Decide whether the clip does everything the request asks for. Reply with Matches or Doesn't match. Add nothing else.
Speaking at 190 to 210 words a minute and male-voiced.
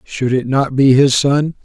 Doesn't match